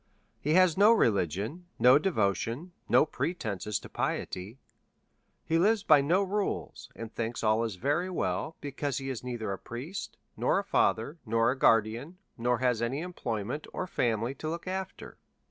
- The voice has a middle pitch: No, low, 130 Hz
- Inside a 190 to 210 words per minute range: No, average, 165 wpm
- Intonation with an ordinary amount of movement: No, wide, 7.0 semitones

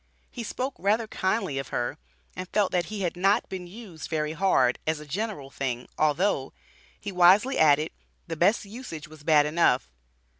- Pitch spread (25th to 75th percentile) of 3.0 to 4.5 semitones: No, average, 5.0 semitones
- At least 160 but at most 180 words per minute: Yes, average, 175 wpm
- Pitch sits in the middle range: Yes, medium, 175 Hz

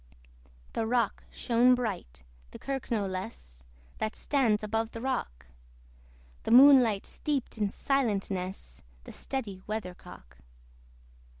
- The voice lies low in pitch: No, high, 220 Hz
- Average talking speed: No, slow, 110 wpm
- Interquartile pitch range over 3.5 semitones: Yes, average, 4.9 semitones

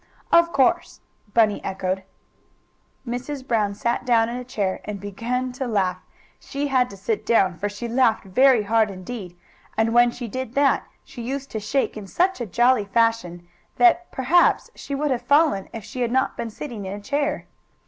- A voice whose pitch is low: No, high, 235 Hz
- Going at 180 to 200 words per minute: Yes, average, 185 wpm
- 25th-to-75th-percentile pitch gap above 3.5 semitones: Yes, average, 4.2 semitones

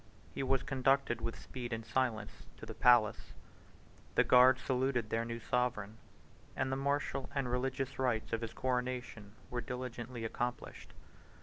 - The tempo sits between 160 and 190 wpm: No, average, 145 wpm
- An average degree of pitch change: No, narrow, 2.2 semitones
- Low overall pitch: Yes, low, 125 Hz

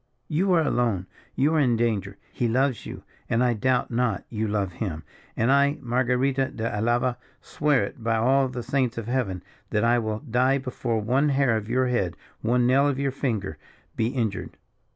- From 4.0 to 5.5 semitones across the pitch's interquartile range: No, average, 3.1 semitones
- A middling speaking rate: Yes, average, 190 wpm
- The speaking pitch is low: Yes, low, 120 Hz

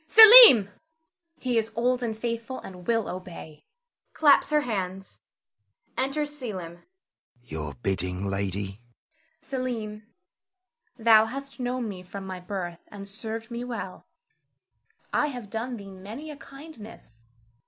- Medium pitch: No, high, 220 Hz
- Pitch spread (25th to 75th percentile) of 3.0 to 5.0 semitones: No, wide, 5.5 semitones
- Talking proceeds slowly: Yes, slow, 130 wpm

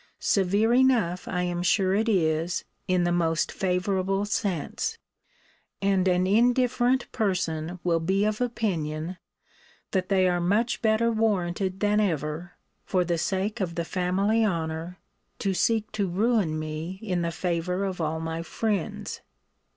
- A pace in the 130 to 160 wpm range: Yes, average, 145 wpm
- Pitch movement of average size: Yes, average, 3.6 semitones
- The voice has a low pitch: No, medium, 185 Hz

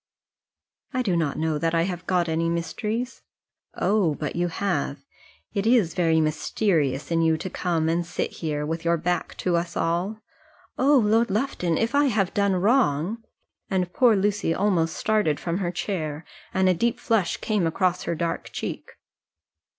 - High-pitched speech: No, medium, 175 Hz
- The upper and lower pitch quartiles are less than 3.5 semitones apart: No, average, 4.1 semitones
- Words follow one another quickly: No, average, 175 wpm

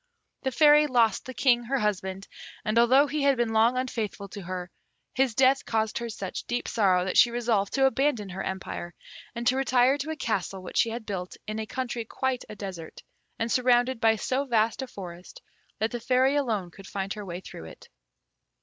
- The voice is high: Yes, high, 230 Hz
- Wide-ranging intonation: No, average, 4.6 semitones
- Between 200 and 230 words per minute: Yes, fast, 205 wpm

